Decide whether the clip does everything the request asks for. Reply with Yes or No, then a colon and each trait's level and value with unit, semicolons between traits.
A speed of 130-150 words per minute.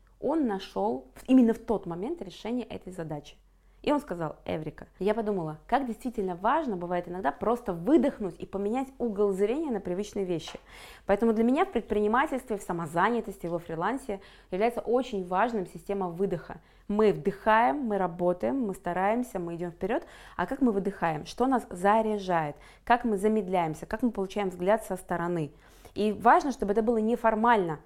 No: fast, 160 wpm